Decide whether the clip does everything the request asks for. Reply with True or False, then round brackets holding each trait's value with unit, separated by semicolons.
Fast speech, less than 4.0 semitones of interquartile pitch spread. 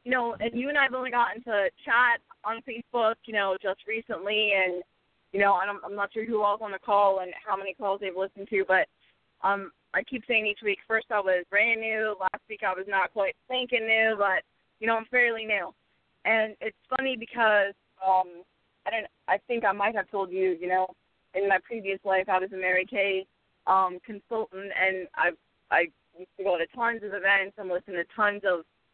True (220 wpm; 2.9 semitones)